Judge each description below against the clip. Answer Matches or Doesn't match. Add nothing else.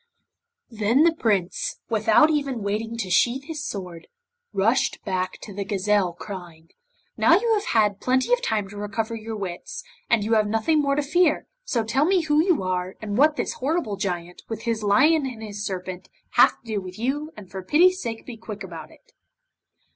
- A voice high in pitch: Matches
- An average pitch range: Doesn't match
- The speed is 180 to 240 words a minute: Matches